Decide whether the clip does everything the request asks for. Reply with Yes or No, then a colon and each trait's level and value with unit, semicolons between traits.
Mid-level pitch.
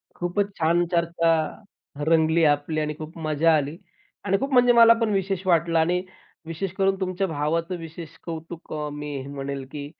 Yes: medium, 165 Hz